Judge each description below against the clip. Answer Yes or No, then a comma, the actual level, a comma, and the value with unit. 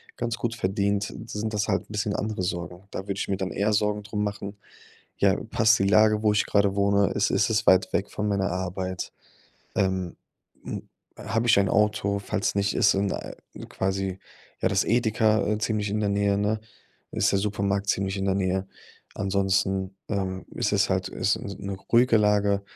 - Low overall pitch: Yes, low, 100 Hz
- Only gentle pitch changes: Yes, narrow, 1.5 semitones